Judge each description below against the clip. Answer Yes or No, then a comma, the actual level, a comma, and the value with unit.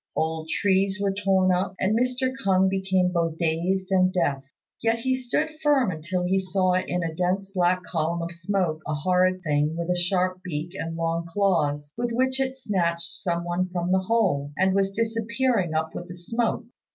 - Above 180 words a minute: Yes, average, 190 wpm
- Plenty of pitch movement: No, average, 2.8 semitones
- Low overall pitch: No, medium, 185 Hz